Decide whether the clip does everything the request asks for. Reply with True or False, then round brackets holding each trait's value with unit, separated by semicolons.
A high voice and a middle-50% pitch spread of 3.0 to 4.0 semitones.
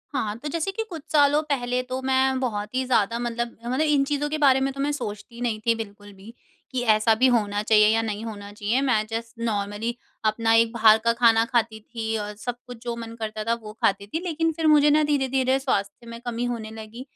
True (235 Hz; 3.5 semitones)